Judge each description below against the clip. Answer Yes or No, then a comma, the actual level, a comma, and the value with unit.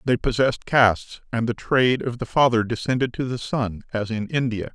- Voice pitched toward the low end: Yes, low, 120 Hz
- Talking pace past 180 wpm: Yes, average, 200 wpm